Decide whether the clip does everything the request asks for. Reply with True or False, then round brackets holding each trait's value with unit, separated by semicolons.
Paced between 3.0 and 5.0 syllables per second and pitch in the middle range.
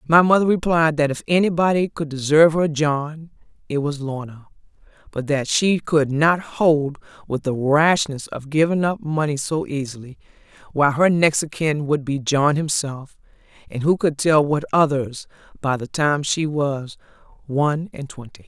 True (4.6 syllables/s; 150 Hz)